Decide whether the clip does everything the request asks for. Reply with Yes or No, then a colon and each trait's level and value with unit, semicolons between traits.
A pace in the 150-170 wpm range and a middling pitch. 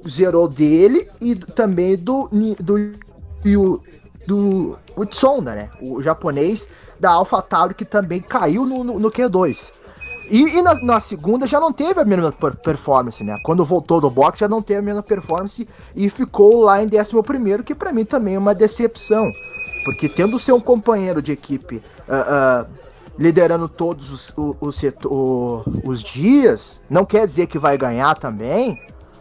No: average, 165 wpm; high, 195 Hz